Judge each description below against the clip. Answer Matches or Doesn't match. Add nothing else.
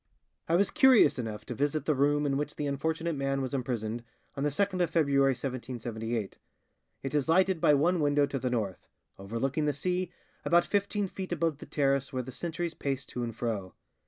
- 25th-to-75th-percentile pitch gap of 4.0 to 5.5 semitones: Matches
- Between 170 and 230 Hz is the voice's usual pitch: Doesn't match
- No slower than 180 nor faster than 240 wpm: Matches